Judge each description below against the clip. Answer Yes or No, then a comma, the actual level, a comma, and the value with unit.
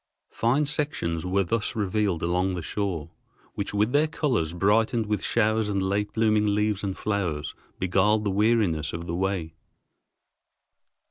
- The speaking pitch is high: No, low, 100 Hz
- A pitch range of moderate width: Yes, average, 3.0 semitones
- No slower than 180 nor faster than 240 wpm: No, average, 145 wpm